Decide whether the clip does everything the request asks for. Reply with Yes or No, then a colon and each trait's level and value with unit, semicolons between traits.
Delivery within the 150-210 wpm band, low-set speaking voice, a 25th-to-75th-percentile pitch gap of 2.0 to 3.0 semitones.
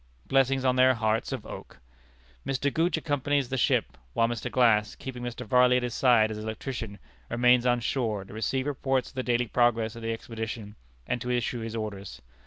Yes: average, 195 wpm; low, 120 Hz; narrow, 2.6 semitones